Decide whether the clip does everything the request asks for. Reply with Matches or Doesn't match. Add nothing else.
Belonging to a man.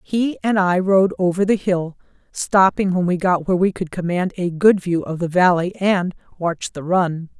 Doesn't match